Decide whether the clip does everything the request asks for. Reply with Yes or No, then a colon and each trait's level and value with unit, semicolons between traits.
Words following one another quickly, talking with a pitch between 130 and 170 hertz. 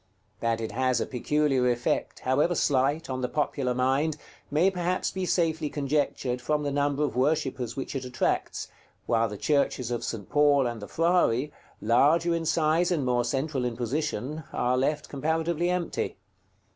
No: average, 165 wpm; medium, 140 Hz